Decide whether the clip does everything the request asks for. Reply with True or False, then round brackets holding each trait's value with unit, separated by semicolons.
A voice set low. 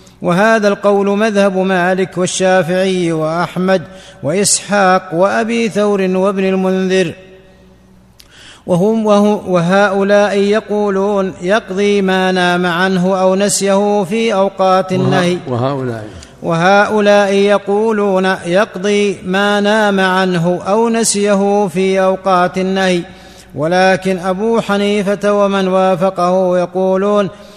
False (190 Hz)